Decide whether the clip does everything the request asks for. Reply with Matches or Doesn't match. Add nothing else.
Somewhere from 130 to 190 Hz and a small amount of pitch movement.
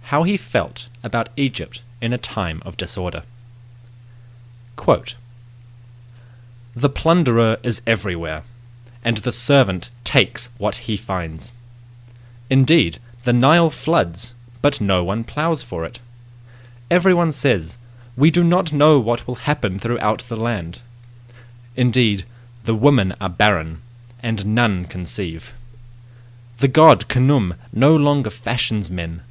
Doesn't match